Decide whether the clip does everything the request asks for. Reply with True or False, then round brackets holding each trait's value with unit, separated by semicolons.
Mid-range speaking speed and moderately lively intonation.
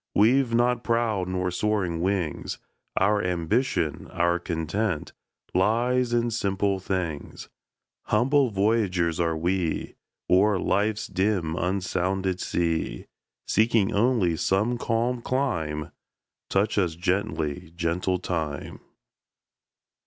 False (100 wpm; 4.4 semitones)